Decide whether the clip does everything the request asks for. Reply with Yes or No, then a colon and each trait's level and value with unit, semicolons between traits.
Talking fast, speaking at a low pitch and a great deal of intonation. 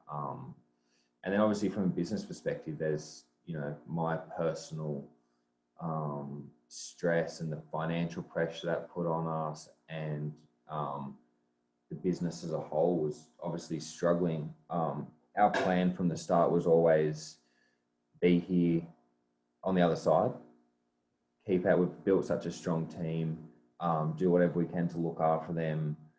No: average, 145 wpm; very low, 80 Hz; wide, 6.0 semitones